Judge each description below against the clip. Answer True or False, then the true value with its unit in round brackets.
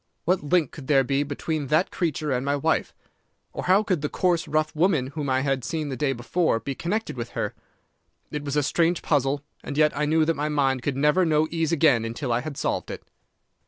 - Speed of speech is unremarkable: False (225 wpm)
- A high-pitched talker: False (150 Hz)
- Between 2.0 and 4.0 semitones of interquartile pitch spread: True (3.0 semitones)